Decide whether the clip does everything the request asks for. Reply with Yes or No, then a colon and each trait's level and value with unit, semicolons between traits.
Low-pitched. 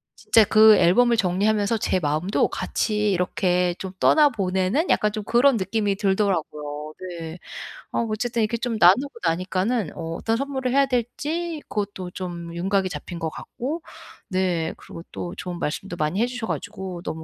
No: high, 200 Hz